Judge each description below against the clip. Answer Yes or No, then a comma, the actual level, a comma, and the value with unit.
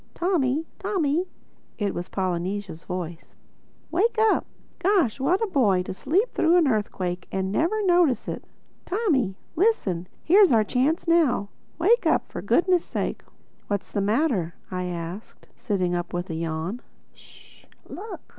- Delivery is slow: Yes, slow, 130 wpm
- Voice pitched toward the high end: Yes, very high, 250 Hz